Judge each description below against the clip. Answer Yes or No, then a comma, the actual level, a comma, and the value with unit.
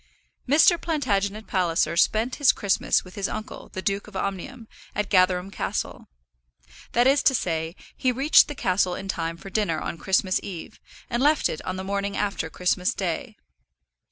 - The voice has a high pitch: Yes, high, 195 Hz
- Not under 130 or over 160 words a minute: No, average, 170 wpm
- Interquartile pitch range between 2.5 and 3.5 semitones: No, average, 4.5 semitones